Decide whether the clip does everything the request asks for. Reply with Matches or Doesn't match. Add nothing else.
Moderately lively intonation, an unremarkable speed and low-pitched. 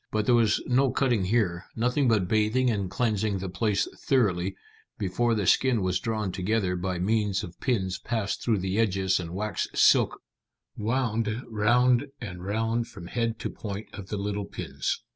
Matches